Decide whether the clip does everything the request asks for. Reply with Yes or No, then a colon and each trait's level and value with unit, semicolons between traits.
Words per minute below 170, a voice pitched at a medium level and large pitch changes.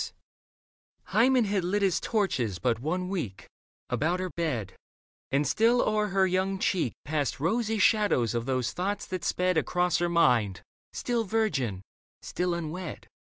Yes: average, 150 wpm; medium, 180 Hz; wide, 6.7 semitones